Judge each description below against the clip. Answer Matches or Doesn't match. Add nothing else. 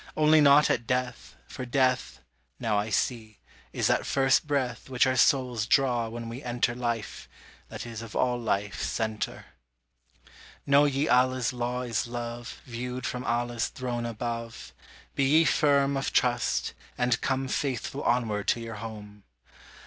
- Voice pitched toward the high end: Doesn't match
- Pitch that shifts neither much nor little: Doesn't match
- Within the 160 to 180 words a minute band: Doesn't match